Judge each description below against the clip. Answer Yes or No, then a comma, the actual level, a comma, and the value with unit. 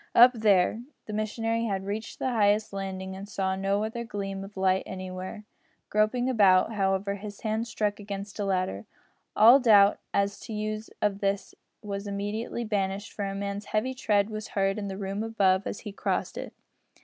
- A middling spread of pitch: No, narrow, 1.7 semitones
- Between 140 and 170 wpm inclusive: No, average, 185 wpm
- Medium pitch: No, high, 205 Hz